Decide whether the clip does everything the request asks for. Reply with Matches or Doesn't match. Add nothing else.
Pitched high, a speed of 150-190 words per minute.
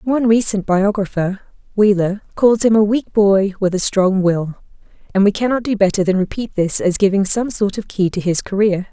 Doesn't match